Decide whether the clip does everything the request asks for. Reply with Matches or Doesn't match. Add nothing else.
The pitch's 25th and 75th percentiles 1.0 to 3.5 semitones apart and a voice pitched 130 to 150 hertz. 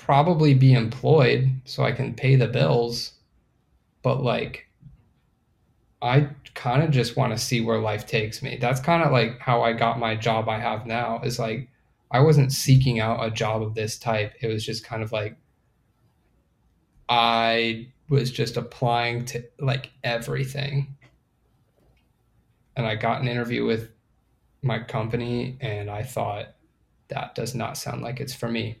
Doesn't match